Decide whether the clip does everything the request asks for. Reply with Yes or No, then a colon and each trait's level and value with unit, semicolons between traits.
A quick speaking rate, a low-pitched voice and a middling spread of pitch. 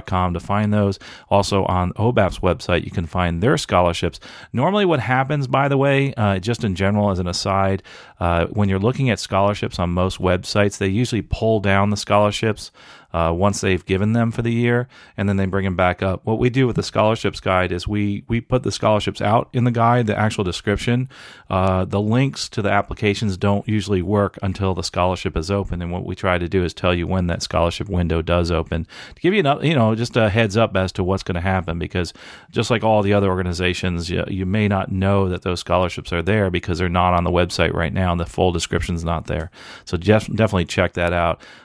Yes: fast, 225 wpm; low, 100 Hz; average, 3.3 semitones